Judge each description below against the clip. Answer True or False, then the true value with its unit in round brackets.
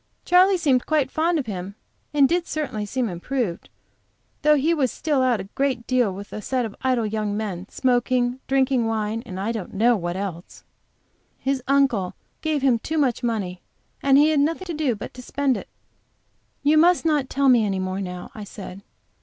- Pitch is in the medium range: False (250 Hz)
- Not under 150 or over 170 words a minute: False (195 wpm)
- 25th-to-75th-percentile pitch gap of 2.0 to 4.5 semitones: False (5.5 semitones)